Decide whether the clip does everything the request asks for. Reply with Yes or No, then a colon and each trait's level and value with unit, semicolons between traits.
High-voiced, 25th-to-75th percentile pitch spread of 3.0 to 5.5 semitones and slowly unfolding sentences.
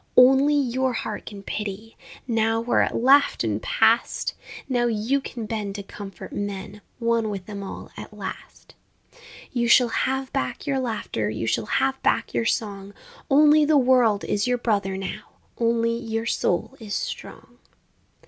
No: high, 230 Hz; average, 4.1 semitones; average, 160 wpm